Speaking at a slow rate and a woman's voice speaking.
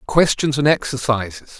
No: slow, 115 wpm; male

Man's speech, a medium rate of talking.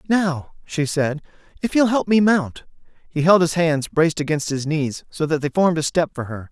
No: male; fast, 220 wpm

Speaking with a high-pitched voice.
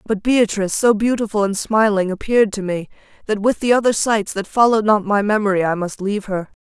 Yes: high, 210 Hz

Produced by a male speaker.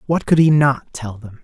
Yes: male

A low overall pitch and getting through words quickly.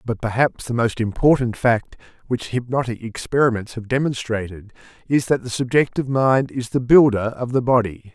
No: low, 120 Hz; average, 160 wpm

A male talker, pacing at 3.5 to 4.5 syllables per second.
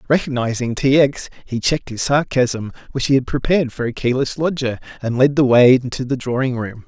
No: male; 5.6 syllables/s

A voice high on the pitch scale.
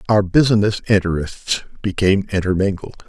No: low, 100 Hz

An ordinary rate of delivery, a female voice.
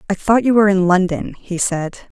No: fast, 220 wpm; female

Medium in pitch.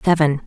Yes: medium, 155 Hz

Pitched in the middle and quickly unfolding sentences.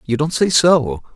Yes: medium, 145 Hz; fast, 210 wpm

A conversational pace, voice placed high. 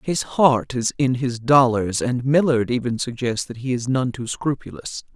No: average, 185 wpm; low, 125 Hz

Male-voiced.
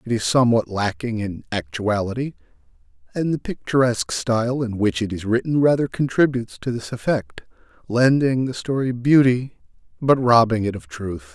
Yes: male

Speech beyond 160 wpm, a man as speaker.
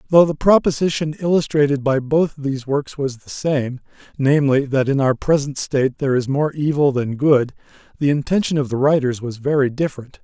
Yes: average, 180 wpm; male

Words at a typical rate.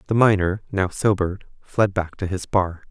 Yes: average, 185 wpm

